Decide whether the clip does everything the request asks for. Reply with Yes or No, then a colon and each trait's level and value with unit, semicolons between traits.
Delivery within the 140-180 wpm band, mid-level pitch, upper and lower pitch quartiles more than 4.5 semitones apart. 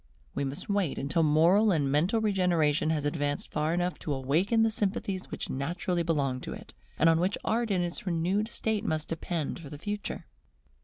No: average, 190 wpm; medium, 170 Hz; average, 5.0 semitones